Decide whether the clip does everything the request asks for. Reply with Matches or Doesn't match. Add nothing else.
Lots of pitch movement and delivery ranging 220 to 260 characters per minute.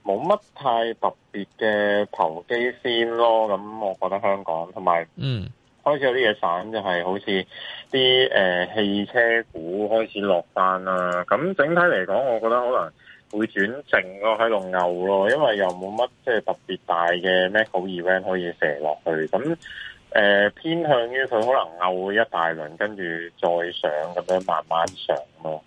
Doesn't match